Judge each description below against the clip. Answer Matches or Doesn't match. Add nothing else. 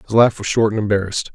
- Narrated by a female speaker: Doesn't match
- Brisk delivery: Matches